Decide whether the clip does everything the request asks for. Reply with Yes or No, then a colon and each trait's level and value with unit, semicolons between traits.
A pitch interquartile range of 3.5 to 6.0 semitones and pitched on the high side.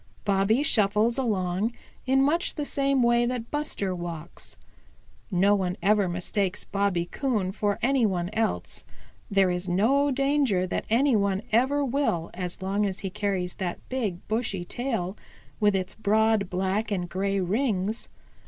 Yes: average, 4.4 semitones; high, 205 Hz